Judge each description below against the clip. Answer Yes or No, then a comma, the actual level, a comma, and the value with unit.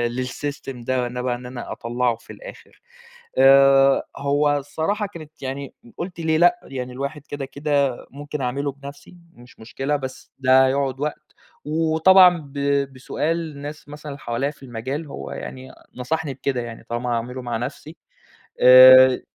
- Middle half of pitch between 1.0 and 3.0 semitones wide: Yes, average, 2.7 semitones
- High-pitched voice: No, low, 135 Hz